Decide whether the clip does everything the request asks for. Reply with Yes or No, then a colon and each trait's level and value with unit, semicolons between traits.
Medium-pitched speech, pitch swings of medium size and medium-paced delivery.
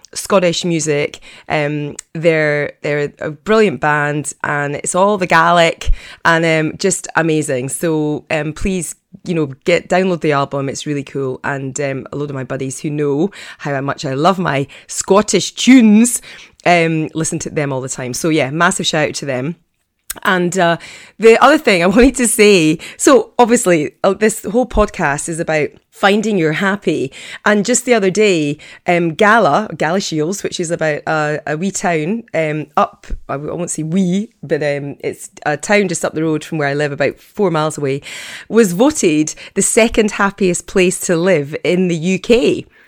Yes: medium, 170 Hz; average, 4.6 semitones; average, 180 wpm